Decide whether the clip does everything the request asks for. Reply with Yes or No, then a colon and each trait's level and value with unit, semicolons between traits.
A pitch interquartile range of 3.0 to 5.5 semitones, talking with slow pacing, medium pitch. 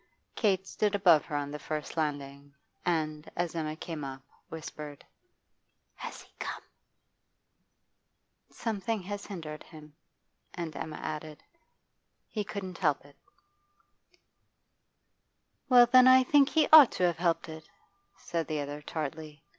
Yes: average, 4.6 semitones; slow, 130 wpm; medium, 160 Hz